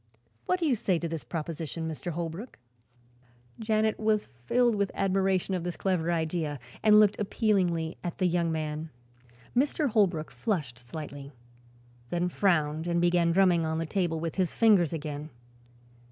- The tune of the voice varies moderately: Yes, average, 3.7 semitones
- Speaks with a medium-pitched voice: Yes, medium, 175 Hz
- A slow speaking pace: No, average, 155 wpm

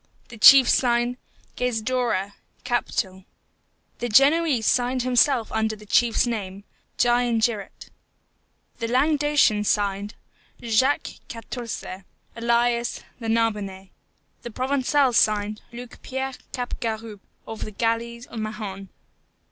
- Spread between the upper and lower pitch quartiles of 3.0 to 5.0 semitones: No, narrow, 2.6 semitones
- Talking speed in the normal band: No, slow, 100 wpm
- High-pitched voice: Yes, high, 235 Hz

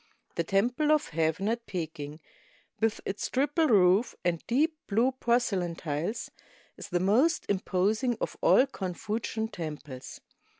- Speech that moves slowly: Yes, slow, 130 wpm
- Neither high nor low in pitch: No, high, 205 Hz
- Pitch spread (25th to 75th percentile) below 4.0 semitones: No, wide, 5.5 semitones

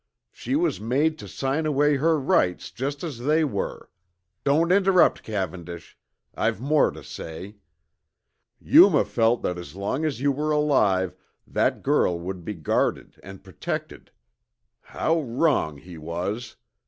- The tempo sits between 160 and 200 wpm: No, average, 140 wpm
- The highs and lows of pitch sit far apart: Yes, wide, 8.4 semitones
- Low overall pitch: Yes, low, 125 Hz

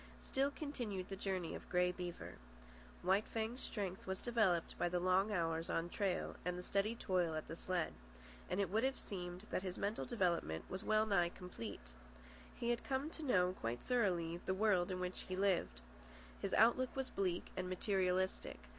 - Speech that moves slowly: No, average, 180 wpm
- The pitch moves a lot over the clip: No, average, 3.4 semitones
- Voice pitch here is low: No, medium, 185 Hz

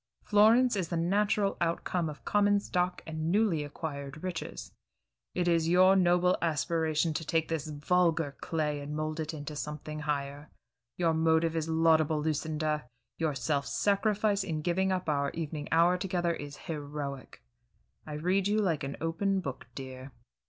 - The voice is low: No, medium, 160 Hz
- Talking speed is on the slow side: No, average, 155 wpm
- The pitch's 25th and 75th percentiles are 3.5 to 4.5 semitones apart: No, average, 3.1 semitones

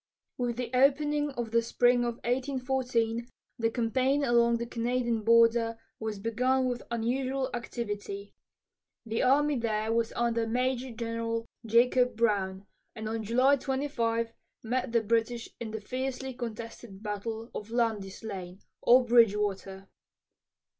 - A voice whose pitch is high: Yes, high, 235 Hz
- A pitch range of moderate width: No, narrow, 2.0 semitones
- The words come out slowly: Yes, slow, 130 wpm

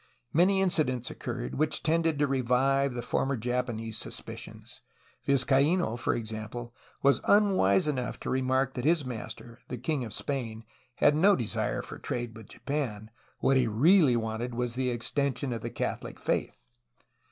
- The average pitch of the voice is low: Yes, low, 125 Hz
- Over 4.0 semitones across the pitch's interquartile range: No, average, 3.6 semitones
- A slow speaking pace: No, average, 160 wpm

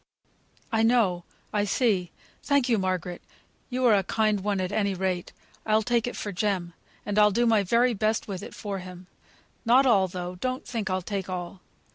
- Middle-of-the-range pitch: No, high, 205 Hz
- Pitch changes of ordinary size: Yes, average, 3.6 semitones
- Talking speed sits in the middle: Yes, average, 185 wpm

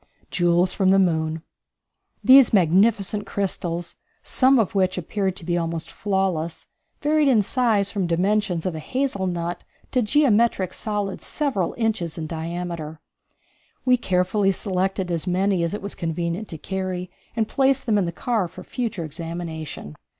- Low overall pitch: No, medium, 185 Hz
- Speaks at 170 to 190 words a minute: No, average, 150 wpm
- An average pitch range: Yes, average, 3.8 semitones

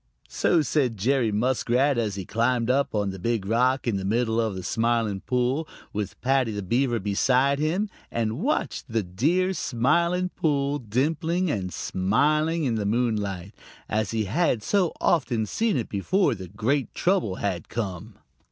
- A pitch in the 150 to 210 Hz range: No, low, 120 Hz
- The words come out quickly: No, average, 160 wpm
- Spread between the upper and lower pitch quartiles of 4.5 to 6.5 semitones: Yes, wide, 5.4 semitones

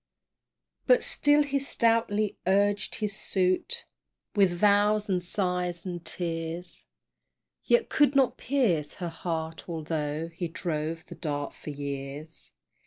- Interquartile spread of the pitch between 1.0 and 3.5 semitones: No, average, 4.4 semitones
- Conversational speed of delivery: No, slow, 120 wpm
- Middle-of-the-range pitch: Yes, medium, 180 Hz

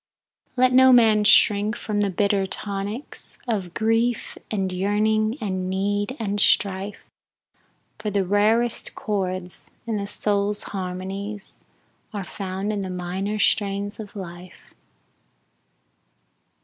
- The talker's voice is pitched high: Yes, high, 205 Hz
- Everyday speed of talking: No, slow, 115 wpm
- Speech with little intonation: Yes, narrow, 1.9 semitones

